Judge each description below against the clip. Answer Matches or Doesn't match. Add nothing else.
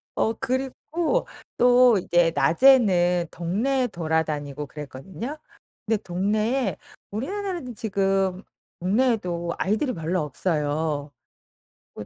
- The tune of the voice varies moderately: Doesn't match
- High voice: Matches